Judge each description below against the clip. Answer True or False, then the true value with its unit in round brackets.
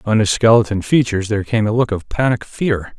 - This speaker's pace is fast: True (220 wpm)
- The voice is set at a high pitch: False (110 Hz)